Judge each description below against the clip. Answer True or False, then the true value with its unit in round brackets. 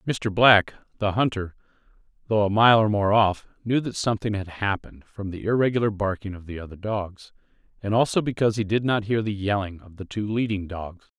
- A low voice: True (105 Hz)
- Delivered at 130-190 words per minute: False (200 wpm)